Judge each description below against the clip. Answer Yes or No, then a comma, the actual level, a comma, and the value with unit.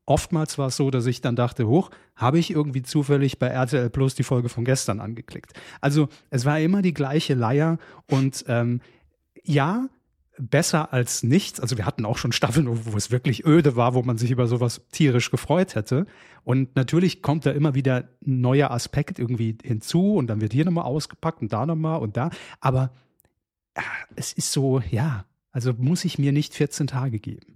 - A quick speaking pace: Yes, fast, 195 wpm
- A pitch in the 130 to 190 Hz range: Yes, low, 135 Hz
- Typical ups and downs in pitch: Yes, average, 3.7 semitones